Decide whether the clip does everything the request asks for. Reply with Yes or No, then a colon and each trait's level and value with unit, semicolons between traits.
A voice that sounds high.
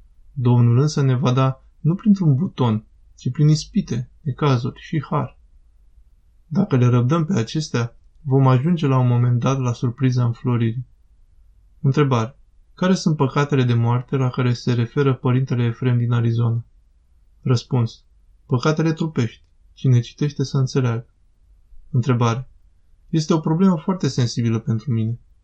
No: low, 125 Hz